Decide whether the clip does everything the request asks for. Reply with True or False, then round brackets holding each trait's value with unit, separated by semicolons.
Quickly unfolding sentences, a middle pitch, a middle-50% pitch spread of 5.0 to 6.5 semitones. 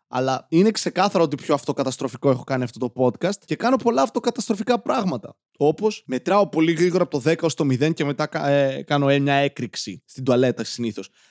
True (185 wpm; 145 Hz; 5.4 semitones)